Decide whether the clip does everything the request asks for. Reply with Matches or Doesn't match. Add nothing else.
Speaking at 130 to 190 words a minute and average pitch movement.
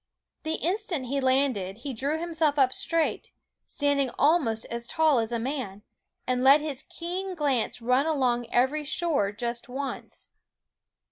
Matches